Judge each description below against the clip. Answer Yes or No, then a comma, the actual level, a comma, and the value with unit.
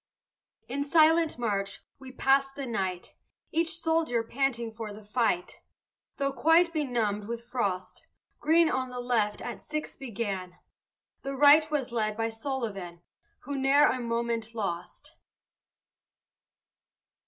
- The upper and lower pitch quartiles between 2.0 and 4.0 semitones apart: No, average, 4.6 semitones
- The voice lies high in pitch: Yes, high, 245 Hz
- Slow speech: Yes, slow, 125 wpm